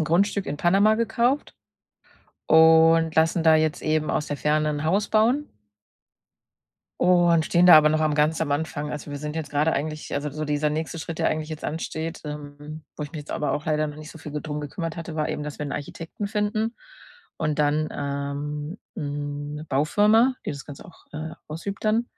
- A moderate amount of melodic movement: No, narrow, 2.0 semitones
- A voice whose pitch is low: No, medium, 155 Hz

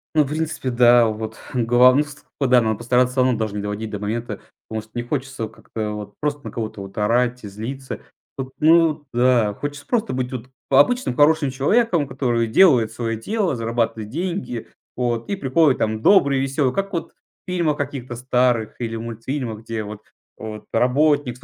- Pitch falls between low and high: No, low, 125 Hz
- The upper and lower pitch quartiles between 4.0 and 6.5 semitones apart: Yes, average, 4.3 semitones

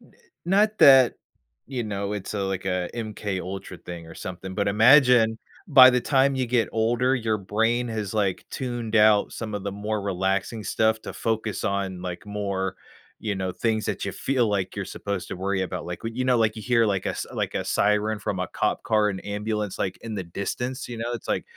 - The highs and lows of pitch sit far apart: No, average, 3.1 semitones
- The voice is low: Yes, low, 105 Hz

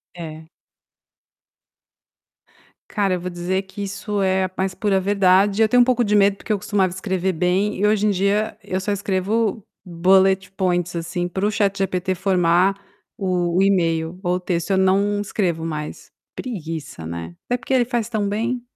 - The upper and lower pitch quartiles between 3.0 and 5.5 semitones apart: No, narrow, 2.5 semitones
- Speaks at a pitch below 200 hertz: Yes, high, 190 Hz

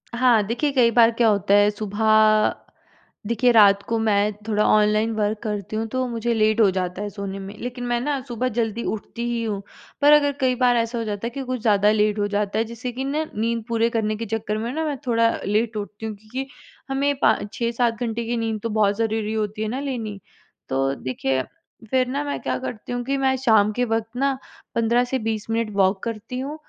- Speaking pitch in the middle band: No, high, 225 Hz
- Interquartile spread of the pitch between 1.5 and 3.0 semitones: Yes, narrow, 2.6 semitones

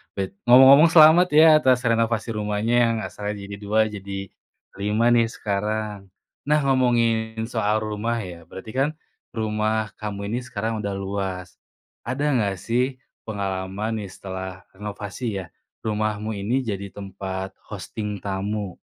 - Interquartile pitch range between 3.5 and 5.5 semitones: No, average, 2.8 semitones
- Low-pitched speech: Yes, low, 105 Hz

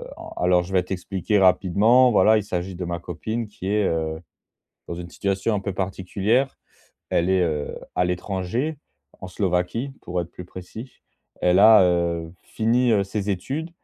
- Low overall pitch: Yes, very low, 95 Hz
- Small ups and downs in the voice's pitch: No, average, 3.3 semitones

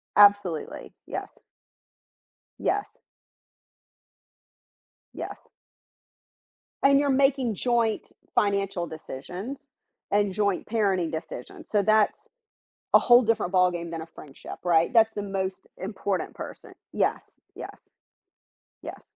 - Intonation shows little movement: No, average, 4.0 semitones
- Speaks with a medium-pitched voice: No, high, 200 Hz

